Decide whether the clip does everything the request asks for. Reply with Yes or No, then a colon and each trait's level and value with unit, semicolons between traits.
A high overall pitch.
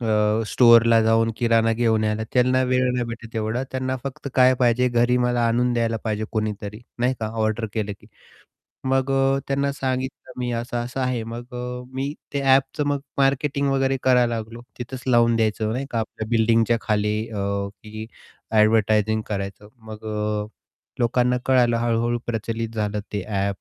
No: low, 115 Hz